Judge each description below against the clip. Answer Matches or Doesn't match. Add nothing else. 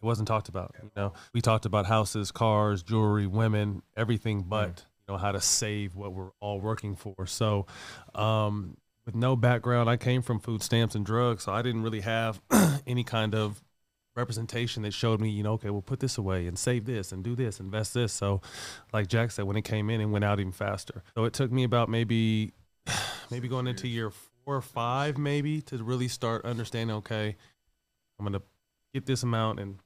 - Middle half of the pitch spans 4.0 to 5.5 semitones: Doesn't match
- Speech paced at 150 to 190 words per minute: Doesn't match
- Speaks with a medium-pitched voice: Doesn't match